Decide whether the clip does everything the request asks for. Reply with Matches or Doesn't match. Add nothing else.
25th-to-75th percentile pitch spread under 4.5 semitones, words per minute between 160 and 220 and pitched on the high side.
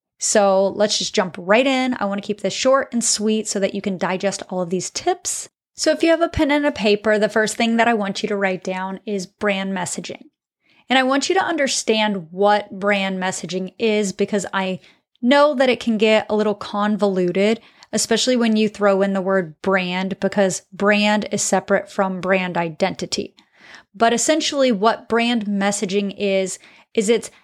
Matches